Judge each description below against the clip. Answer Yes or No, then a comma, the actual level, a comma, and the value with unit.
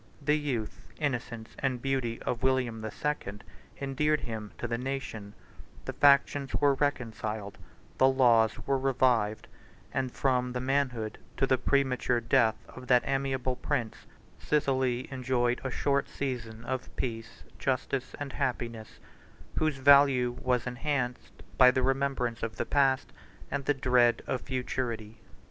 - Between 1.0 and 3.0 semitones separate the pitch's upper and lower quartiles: Yes, narrow, 2.5 semitones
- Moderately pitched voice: No, low, 130 Hz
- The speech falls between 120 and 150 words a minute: Yes, average, 140 wpm